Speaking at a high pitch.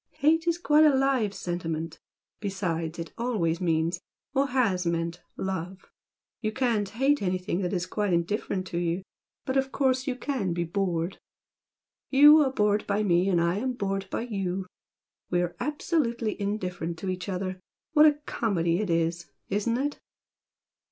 Yes: high, 195 Hz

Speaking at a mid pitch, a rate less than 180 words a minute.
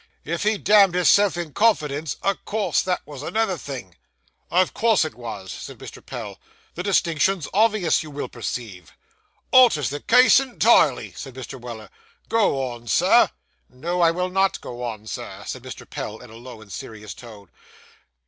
Yes: medium, 155 Hz; average, 165 wpm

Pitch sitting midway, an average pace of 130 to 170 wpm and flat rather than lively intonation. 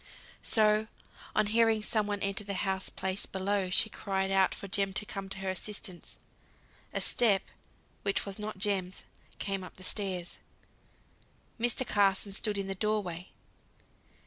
No: high, 195 Hz; average, 155 wpm; narrow, 1.7 semitones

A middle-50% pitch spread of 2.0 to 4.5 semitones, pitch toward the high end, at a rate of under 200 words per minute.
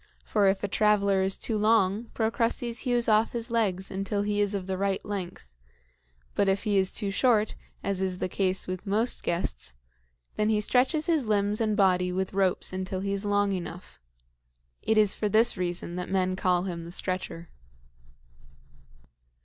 Yes: narrow, 2.4 semitones; high, 200 Hz; average, 175 wpm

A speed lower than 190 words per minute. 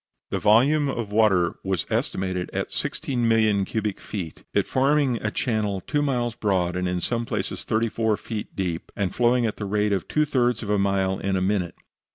No: average, 195 wpm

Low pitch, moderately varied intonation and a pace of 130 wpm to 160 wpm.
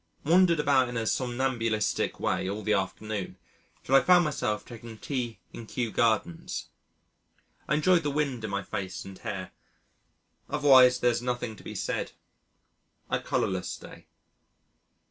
Yes: low, 120 Hz; average, 4.2 semitones; average, 145 wpm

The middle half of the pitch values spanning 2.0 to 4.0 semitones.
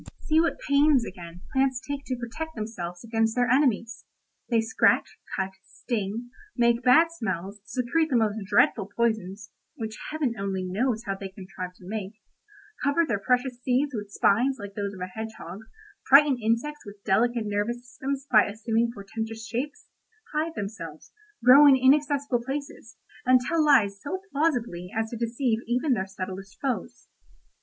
No: average, 4.7 semitones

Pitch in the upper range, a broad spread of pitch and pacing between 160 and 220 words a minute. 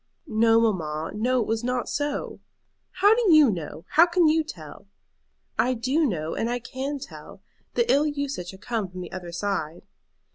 Yes: high, 240 Hz; wide, 7.9 semitones; average, 180 wpm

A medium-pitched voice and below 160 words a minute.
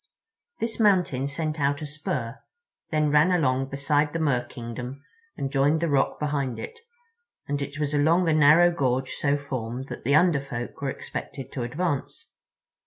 No: medium, 145 Hz; average, 165 wpm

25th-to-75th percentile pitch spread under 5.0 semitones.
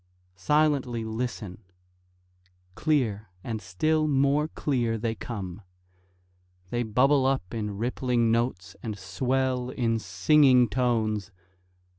Yes: average, 3.7 semitones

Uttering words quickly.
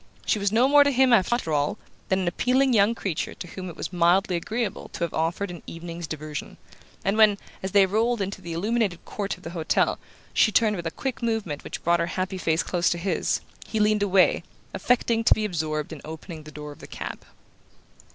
Yes: fast, 215 wpm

